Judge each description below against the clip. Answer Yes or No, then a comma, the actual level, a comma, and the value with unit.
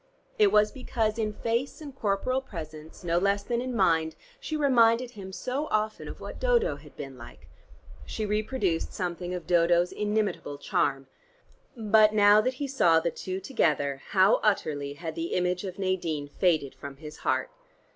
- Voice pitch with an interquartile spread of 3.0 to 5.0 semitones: No, wide, 5.4 semitones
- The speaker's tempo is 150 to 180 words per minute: Yes, average, 165 wpm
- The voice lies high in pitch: Yes, high, 200 Hz